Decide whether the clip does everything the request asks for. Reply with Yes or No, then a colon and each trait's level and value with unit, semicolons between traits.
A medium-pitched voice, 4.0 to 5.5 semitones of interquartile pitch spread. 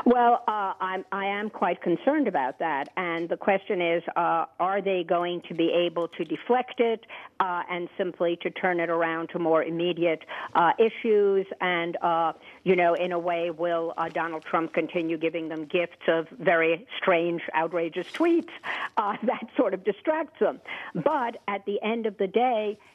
No: medium, 180 Hz; average, 3.5 semitones